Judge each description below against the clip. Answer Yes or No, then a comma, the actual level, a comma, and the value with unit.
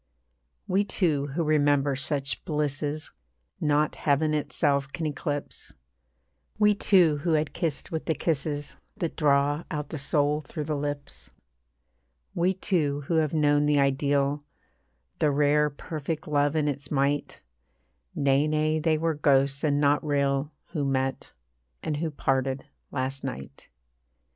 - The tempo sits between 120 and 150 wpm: Yes, average, 140 wpm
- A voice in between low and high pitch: Yes, medium, 145 Hz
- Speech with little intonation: Yes, narrow, 1.6 semitones